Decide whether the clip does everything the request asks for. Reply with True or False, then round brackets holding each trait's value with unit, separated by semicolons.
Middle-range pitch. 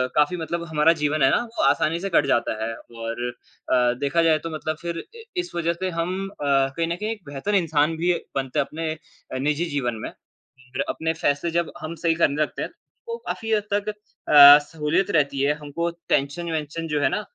True (155 Hz)